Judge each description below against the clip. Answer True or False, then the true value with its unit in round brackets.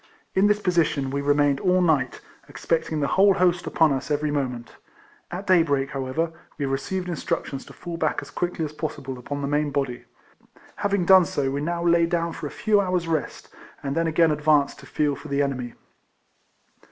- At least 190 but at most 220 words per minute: True (200 wpm)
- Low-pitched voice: False (155 Hz)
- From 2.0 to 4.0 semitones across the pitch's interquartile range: True (3.7 semitones)